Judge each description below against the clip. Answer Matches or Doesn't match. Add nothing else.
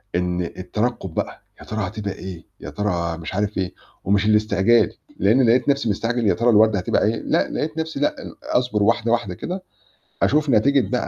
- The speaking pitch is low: Matches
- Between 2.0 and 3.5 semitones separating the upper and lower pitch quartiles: Doesn't match